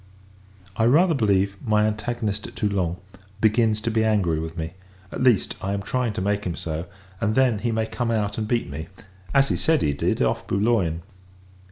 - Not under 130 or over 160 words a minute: No, average, 195 wpm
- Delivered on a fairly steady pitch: No, average, 3.4 semitones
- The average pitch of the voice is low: Yes, low, 105 Hz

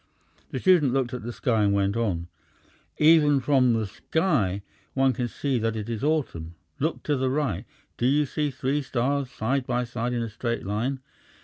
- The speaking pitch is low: Yes, low, 125 Hz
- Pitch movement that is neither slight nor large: Yes, average, 3.9 semitones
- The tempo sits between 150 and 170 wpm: No, average, 190 wpm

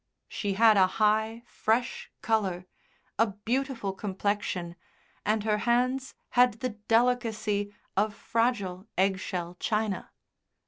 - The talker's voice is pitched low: No, high, 215 Hz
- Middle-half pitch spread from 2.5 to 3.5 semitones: Yes, average, 2.8 semitones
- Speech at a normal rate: No, slow, 110 wpm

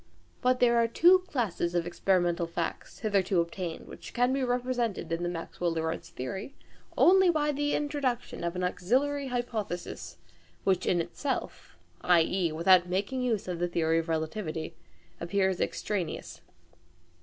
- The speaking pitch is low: No, high, 190 Hz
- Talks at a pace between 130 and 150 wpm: Yes, average, 145 wpm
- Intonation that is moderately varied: No, wide, 6.5 semitones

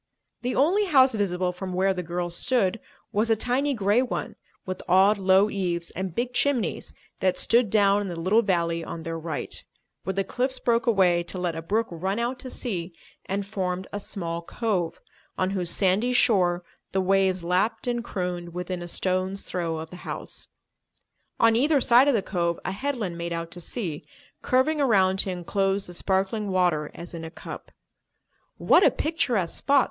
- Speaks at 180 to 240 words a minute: Yes, average, 185 wpm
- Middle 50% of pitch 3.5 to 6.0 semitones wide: Yes, average, 4.6 semitones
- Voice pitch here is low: No, high, 190 Hz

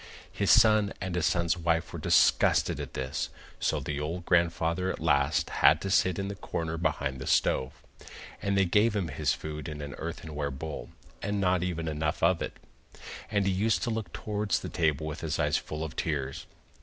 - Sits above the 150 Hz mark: No, very low, 85 Hz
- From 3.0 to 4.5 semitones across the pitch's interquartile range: Yes, average, 3.7 semitones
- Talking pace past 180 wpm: Yes, average, 195 wpm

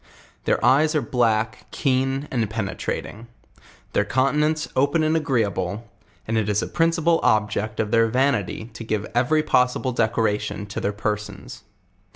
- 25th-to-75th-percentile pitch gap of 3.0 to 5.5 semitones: Yes, average, 4.4 semitones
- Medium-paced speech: Yes, average, 150 wpm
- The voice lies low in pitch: Yes, low, 115 Hz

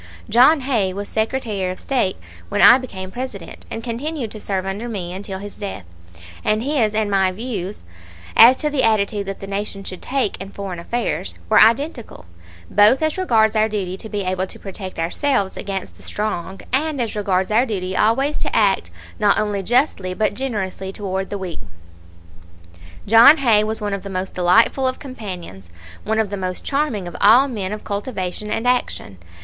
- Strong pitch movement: No, average, 4.0 semitones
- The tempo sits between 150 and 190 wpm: Yes, average, 185 wpm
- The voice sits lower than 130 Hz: No, high, 210 Hz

